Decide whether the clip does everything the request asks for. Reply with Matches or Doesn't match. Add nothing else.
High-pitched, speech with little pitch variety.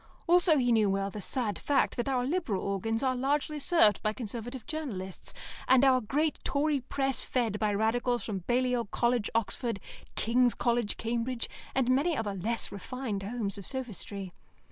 Doesn't match